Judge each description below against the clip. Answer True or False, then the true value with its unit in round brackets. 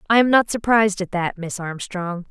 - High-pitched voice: True (195 Hz)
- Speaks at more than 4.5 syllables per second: True (5.2 syllables/s)